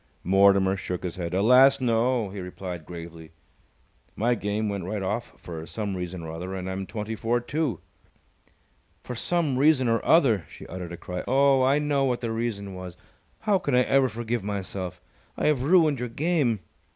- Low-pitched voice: Yes, low, 110 Hz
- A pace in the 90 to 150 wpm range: No, average, 180 wpm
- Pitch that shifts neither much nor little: No, wide, 5.7 semitones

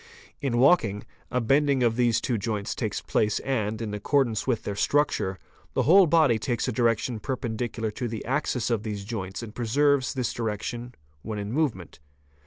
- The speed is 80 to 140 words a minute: No, average, 175 wpm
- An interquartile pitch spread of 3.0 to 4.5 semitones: Yes, average, 3.6 semitones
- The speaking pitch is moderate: No, low, 115 Hz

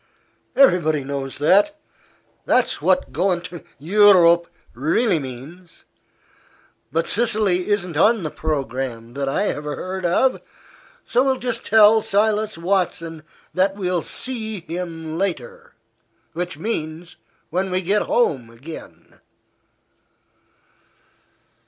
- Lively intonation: No, average, 4.9 semitones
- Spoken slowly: Yes, slow, 110 wpm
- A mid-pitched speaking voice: Yes, medium, 180 Hz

